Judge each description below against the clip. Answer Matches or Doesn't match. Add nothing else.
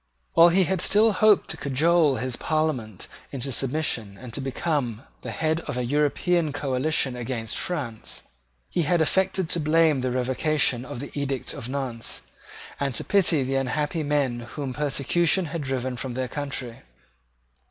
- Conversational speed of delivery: Matches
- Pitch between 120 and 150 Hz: Matches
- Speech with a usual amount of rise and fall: Matches